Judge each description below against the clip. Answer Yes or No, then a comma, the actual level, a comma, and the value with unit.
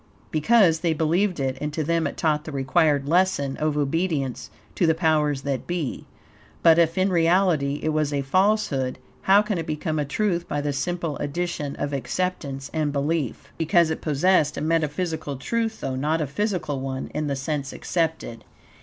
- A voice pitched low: No, medium, 155 Hz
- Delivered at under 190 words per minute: Yes, average, 180 wpm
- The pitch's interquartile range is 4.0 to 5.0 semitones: No, average, 3.4 semitones